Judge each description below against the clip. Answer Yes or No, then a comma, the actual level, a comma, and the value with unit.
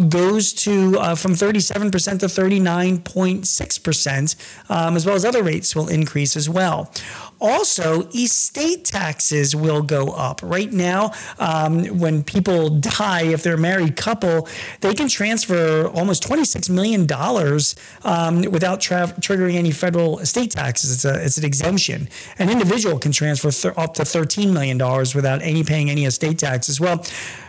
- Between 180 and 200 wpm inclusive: No, average, 160 wpm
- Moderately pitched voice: Yes, medium, 170 Hz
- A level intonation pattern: No, average, 4.0 semitones